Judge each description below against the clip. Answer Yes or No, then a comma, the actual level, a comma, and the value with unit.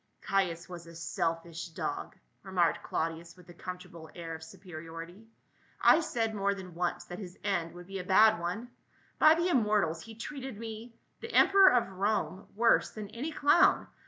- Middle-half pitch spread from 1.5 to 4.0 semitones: No, average, 4.7 semitones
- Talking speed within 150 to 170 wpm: No, average, 190 wpm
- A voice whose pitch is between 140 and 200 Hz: Yes, high, 190 Hz